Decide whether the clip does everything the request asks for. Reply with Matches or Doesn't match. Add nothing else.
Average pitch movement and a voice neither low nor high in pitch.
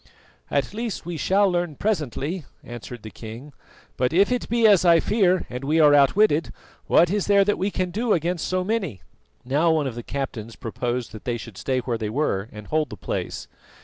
Doesn't match